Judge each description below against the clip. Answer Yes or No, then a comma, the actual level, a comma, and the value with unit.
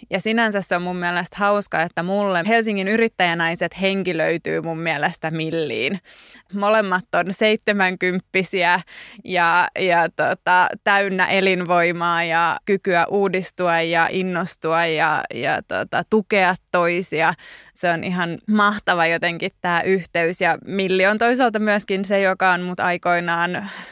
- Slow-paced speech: Yes, slow, 130 wpm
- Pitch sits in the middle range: Yes, medium, 180 Hz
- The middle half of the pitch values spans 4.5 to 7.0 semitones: No, average, 2.7 semitones